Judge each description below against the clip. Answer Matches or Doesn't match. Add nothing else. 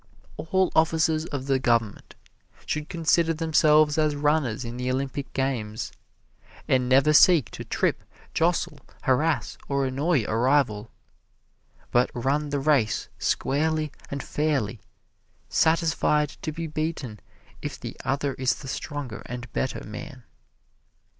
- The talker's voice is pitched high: Doesn't match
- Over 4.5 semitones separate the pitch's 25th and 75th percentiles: Doesn't match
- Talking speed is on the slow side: Matches